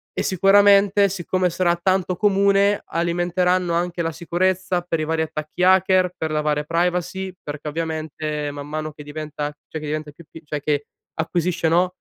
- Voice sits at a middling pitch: Yes, medium, 170 Hz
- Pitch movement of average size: Yes, average, 3.1 semitones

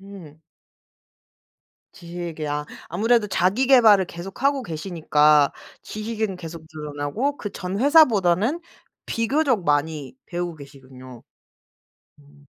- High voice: No, medium, 175 Hz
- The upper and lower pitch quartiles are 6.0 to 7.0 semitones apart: Yes, wide, 6.7 semitones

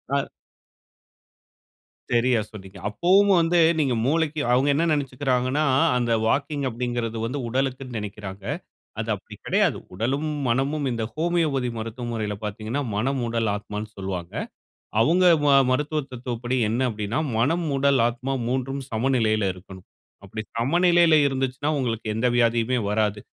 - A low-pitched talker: Yes, low, 125 Hz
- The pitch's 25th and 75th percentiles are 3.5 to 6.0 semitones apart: Yes, average, 4.0 semitones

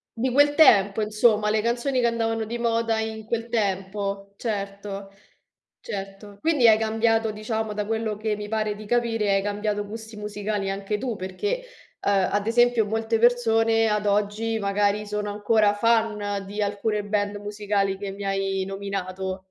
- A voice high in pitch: Yes, high, 210 Hz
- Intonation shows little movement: Yes, narrow, 1.9 semitones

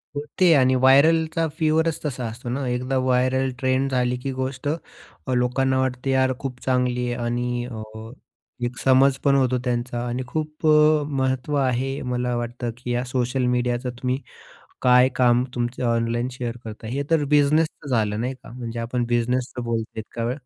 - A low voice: Yes, low, 125 Hz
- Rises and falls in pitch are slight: Yes, narrow, 1.8 semitones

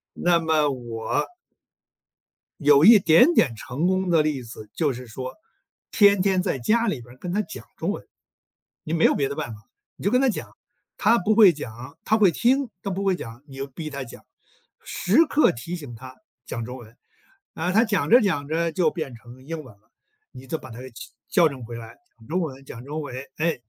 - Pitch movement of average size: No, wide, 6.7 semitones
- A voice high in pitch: No, medium, 150 Hz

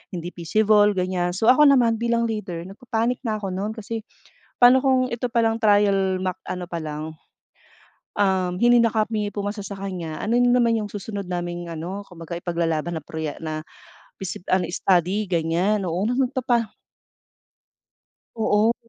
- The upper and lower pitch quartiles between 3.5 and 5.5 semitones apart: Yes, average, 4.5 semitones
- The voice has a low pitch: No, high, 200 Hz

